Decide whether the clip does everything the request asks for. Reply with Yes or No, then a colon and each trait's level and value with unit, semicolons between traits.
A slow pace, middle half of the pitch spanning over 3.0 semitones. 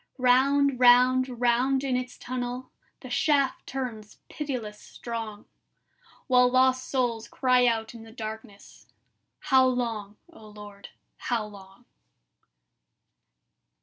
No: slow, 110 wpm; narrow, 2.6 semitones